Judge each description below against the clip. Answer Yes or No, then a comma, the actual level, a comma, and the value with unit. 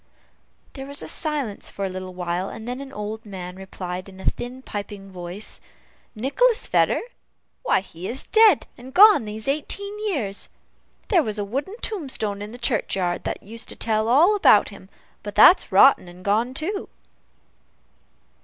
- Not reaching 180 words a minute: Yes, average, 165 wpm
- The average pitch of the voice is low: No, high, 220 Hz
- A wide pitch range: Yes, wide, 6.2 semitones